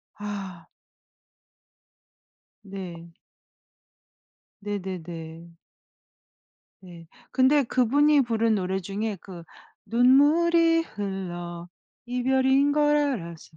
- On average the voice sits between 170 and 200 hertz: No, high, 210 Hz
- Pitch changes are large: Yes, wide, 7.0 semitones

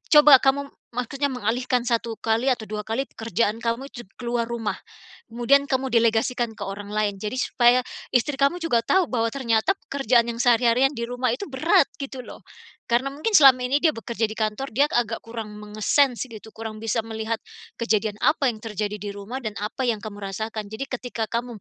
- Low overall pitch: No, high, 235 Hz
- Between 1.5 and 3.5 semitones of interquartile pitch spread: Yes, average, 3.1 semitones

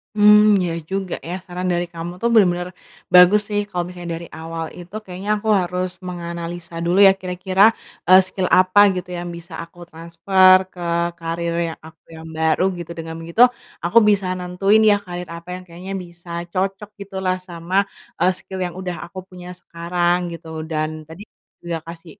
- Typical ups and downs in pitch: No, narrow, 1.8 semitones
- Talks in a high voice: No, medium, 180 Hz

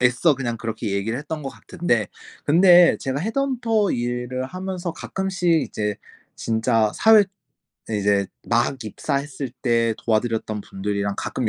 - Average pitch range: No, wide, 7.7 semitones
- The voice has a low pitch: Yes, low, 125 Hz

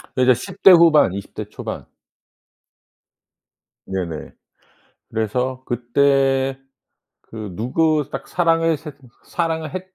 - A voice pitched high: No, low, 135 Hz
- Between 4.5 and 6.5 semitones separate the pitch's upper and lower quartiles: Yes, average, 5.2 semitones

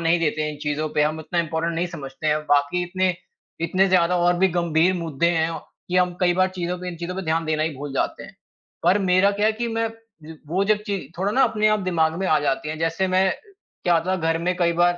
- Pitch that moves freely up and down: No, average, 2.7 semitones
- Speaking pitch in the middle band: Yes, medium, 175 Hz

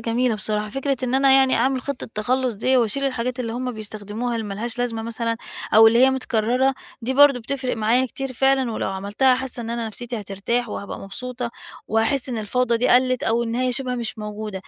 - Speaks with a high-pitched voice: Yes, high, 240 Hz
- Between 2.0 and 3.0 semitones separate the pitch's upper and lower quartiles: Yes, narrow, 2.6 semitones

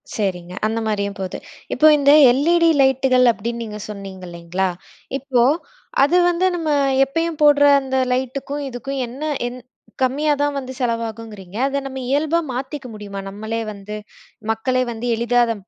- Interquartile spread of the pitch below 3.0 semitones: No, average, 4.8 semitones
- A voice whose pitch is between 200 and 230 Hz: No, very high, 250 Hz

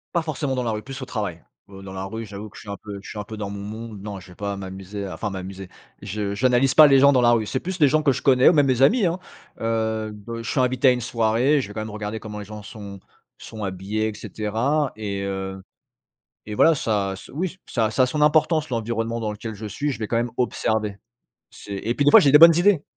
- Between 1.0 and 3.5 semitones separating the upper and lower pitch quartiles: No, average, 4.5 semitones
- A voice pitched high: No, low, 110 Hz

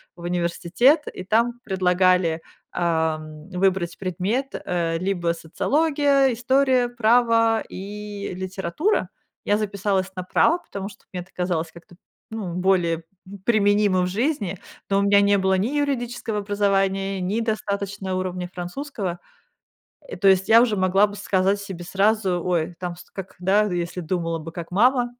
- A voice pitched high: Yes, high, 195 Hz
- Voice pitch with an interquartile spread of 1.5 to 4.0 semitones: Yes, average, 3.3 semitones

